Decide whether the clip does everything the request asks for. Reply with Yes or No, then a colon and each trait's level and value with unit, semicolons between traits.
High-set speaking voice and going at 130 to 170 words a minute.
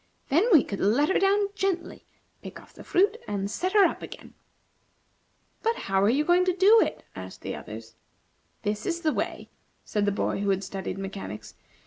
No: very high, 285 Hz; average, 190 wpm